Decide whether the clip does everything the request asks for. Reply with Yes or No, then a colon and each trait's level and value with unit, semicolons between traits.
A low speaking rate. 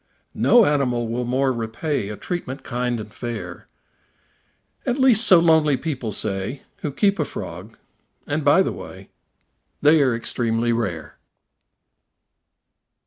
Yes: slow, 130 wpm